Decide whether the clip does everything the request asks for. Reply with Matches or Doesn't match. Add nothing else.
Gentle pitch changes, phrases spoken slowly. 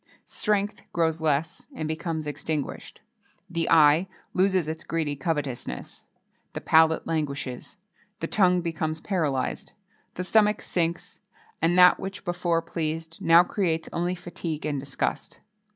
Matches